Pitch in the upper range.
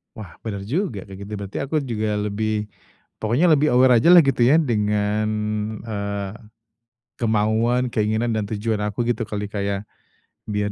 No: low, 110 Hz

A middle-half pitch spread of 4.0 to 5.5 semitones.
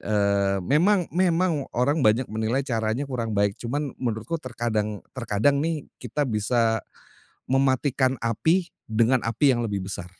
Yes: average, 4.7 semitones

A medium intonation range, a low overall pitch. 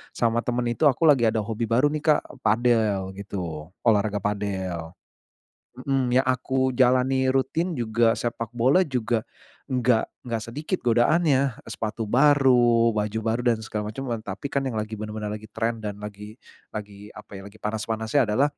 Yes: average, 3.4 semitones; low, 115 Hz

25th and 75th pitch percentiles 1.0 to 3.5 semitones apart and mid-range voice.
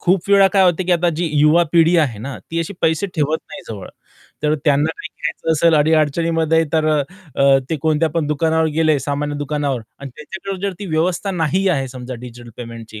Yes: average, 2.8 semitones; medium, 155 Hz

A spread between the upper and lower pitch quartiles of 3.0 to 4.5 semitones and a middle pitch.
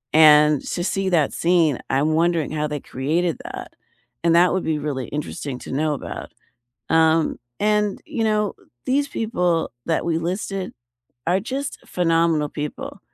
Yes: average, 3.8 semitones; medium, 165 Hz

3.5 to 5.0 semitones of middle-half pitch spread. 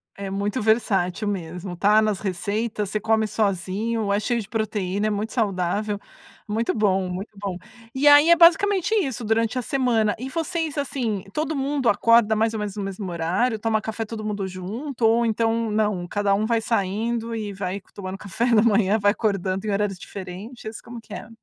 No: average, 2.7 semitones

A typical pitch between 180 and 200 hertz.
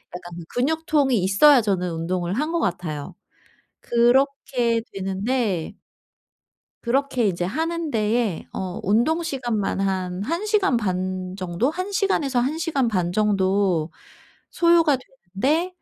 No: high, 230 Hz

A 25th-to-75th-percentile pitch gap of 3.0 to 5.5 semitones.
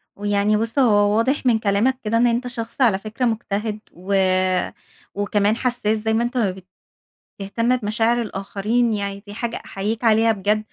No: narrow, 2.4 semitones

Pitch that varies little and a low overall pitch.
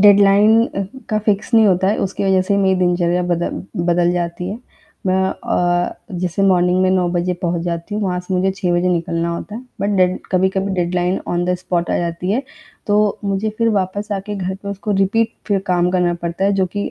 No: narrow, 2.2 semitones; medium, 185 Hz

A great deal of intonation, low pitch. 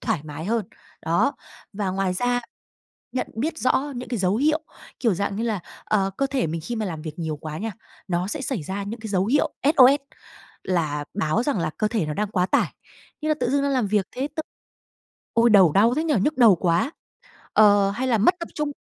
No: wide, 5.8 semitones; high, 215 Hz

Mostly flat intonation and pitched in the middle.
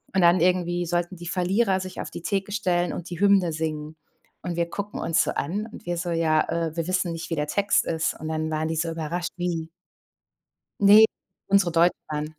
Yes: narrow, 2.3 semitones; medium, 175 Hz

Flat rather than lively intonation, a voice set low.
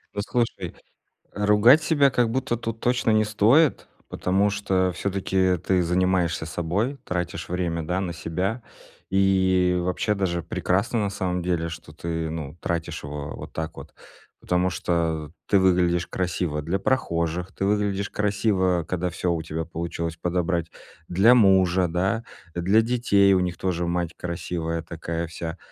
No: average, 3.0 semitones; very low, 90 Hz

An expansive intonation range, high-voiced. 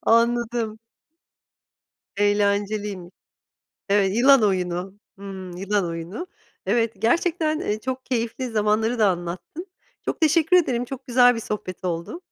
No: average, 4.1 semitones; high, 215 Hz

